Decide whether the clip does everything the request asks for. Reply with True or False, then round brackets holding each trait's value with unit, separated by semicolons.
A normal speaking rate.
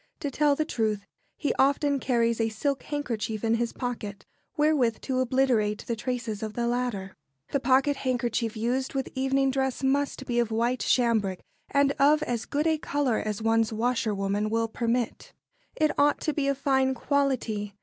True (170 wpm)